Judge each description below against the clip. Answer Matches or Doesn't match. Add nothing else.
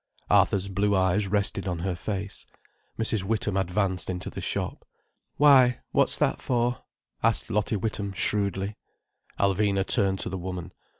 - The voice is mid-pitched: Doesn't match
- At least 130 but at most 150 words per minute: Matches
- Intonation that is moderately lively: Doesn't match